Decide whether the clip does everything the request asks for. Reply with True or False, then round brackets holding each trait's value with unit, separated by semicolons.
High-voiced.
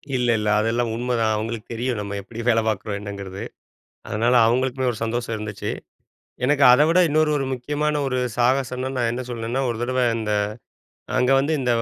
False (120 Hz)